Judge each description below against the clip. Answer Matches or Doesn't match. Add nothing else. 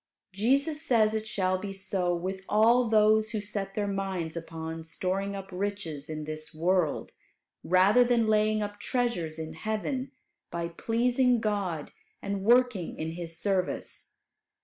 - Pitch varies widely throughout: Doesn't match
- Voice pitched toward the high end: Matches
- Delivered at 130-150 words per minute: Matches